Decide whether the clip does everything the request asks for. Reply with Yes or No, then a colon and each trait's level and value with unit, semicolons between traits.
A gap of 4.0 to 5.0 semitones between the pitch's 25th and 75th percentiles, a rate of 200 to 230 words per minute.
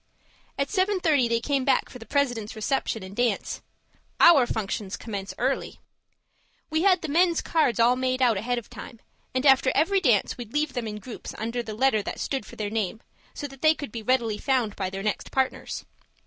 Yes: average, 4.4 semitones; fast, 205 wpm